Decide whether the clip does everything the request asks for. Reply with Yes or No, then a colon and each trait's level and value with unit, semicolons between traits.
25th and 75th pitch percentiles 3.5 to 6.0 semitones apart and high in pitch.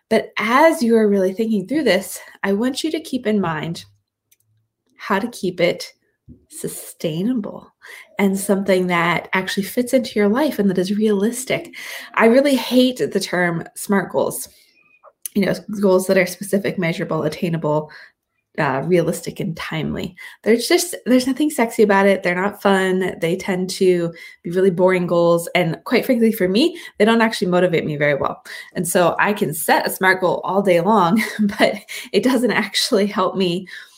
Yes: average, 4.0 semitones; high, 195 Hz